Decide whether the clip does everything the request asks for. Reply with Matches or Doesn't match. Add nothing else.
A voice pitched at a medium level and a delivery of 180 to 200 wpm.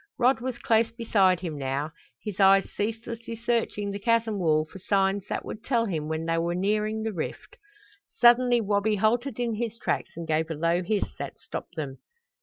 Doesn't match